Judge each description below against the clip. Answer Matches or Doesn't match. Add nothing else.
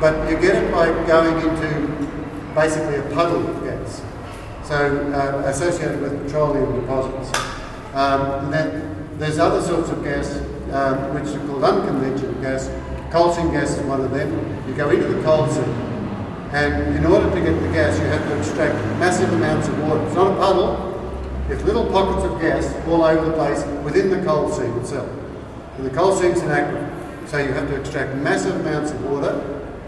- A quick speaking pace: Doesn't match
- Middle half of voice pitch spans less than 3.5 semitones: Matches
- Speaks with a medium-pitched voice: Matches